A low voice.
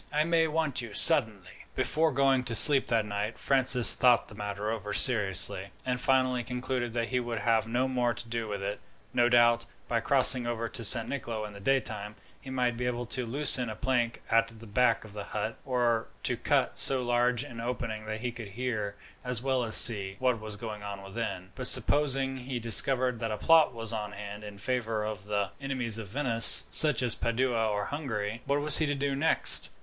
Yes: low, 120 Hz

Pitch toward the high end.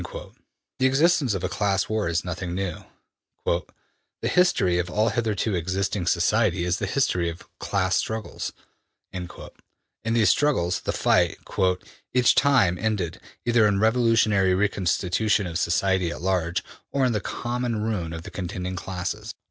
No: very low, 95 Hz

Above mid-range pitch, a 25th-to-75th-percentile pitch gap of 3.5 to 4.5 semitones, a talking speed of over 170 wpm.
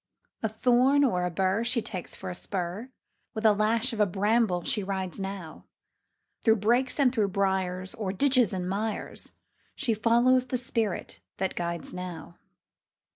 No: high, 210 Hz; average, 4.0 semitones; average, 160 wpm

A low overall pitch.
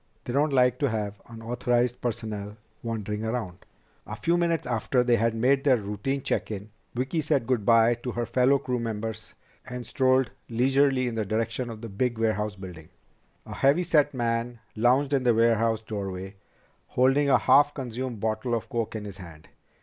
Yes: low, 120 Hz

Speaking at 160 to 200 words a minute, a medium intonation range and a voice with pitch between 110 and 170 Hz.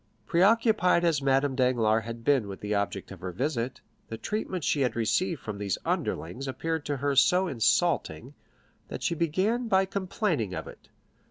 No: average, 170 wpm; wide, 8.1 semitones; low, 135 Hz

